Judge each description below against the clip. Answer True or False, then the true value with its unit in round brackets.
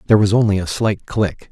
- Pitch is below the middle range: True (105 Hz)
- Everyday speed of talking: False (235 wpm)